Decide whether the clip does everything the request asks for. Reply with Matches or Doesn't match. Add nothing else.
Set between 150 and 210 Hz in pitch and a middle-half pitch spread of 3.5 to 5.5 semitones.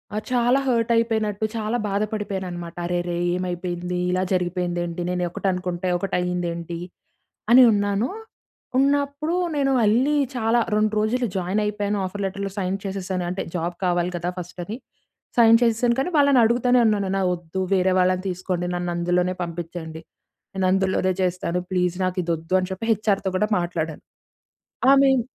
Matches